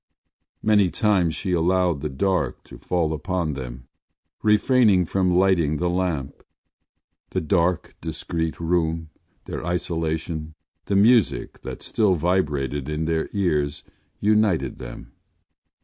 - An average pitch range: Yes, average, 3.3 semitones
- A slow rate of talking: Yes, slow, 115 wpm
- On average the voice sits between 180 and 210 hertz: No, very low, 85 Hz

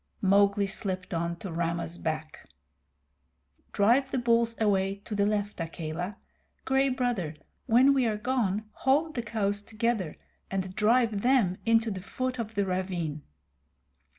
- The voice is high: Yes, high, 205 Hz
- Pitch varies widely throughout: No, average, 4.1 semitones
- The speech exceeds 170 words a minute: No, average, 140 wpm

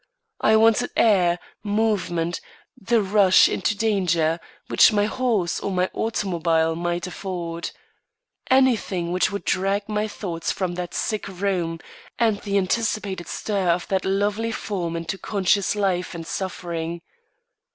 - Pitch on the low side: No, high, 190 Hz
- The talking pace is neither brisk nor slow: No, slow, 130 wpm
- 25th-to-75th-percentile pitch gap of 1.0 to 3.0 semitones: No, average, 3.4 semitones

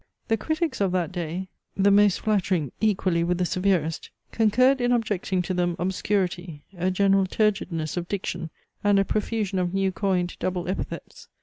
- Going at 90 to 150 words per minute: No, average, 165 wpm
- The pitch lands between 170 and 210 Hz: Yes, high, 190 Hz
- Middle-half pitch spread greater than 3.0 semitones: No, narrow, 2.6 semitones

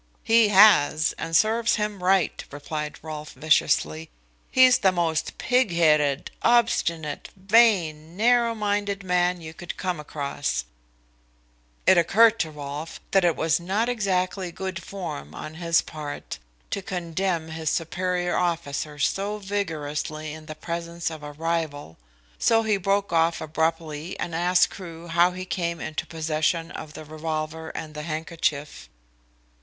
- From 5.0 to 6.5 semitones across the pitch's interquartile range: No, average, 3.7 semitones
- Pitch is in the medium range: Yes, medium, 170 Hz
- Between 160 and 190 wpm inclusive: No, average, 140 wpm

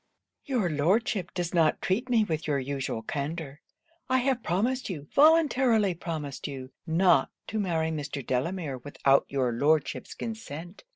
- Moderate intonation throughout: No, wide, 7.2 semitones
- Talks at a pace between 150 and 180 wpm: No, average, 140 wpm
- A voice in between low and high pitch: Yes, medium, 165 Hz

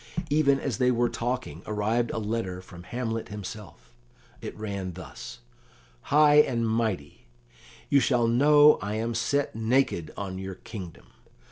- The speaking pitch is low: Yes, low, 110 Hz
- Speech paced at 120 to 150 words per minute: Yes, average, 140 wpm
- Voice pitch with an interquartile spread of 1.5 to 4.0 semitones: No, average, 4.6 semitones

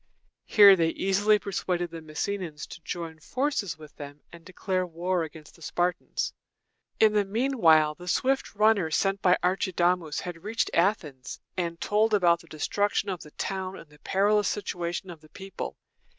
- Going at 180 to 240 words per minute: No, average, 165 wpm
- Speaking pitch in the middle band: Yes, medium, 180 Hz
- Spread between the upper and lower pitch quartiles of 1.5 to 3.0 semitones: No, average, 3.6 semitones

